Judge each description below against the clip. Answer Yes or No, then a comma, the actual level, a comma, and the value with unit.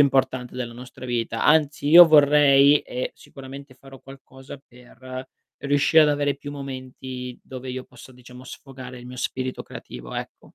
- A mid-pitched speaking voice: No, low, 130 Hz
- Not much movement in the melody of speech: Yes, narrow, 1.9 semitones